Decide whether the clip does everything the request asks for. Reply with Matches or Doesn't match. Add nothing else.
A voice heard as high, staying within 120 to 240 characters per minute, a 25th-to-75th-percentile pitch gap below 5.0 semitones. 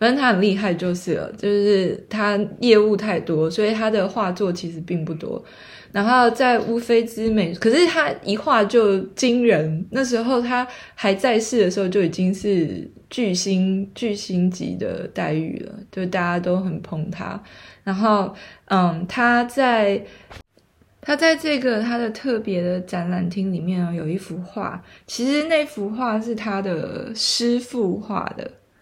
Matches